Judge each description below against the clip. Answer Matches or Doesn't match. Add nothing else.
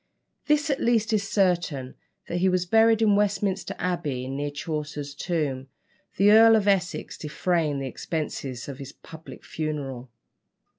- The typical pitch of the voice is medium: Matches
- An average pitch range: Doesn't match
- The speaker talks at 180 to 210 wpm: Doesn't match